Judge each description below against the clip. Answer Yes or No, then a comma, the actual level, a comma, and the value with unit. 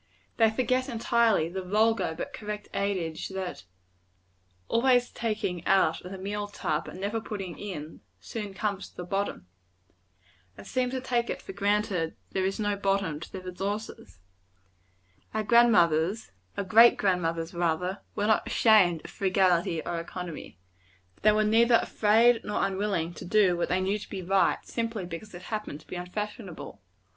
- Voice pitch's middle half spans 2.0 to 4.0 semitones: Yes, average, 3.4 semitones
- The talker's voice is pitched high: Yes, high, 195 Hz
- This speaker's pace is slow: No, average, 165 wpm